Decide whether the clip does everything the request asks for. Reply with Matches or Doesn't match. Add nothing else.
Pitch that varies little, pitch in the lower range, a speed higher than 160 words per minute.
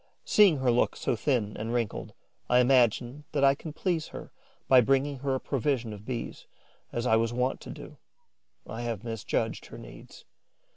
Doesn't match